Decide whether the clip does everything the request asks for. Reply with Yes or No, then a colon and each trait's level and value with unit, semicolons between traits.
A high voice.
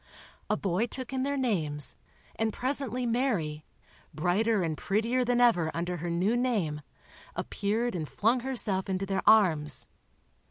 Yes: high, 210 Hz